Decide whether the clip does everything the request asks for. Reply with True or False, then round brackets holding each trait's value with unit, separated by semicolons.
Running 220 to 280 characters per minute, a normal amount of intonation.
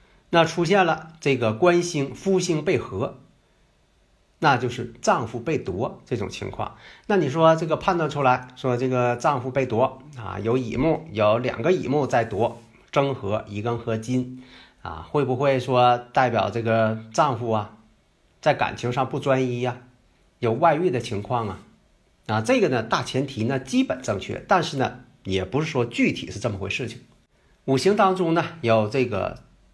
True (240 characters per minute; 4.7 semitones)